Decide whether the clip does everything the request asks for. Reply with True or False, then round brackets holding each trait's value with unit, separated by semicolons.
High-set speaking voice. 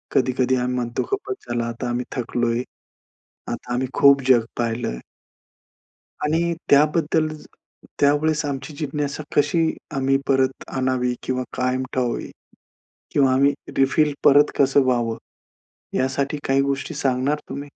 False (135 Hz)